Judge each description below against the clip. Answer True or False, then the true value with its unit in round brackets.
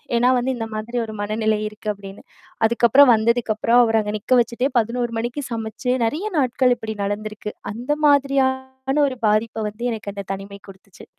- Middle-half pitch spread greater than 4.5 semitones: False (2.8 semitones)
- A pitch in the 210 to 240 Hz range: True (230 Hz)